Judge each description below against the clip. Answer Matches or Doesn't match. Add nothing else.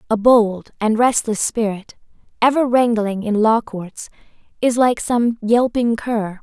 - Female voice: Matches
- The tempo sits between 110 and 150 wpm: Matches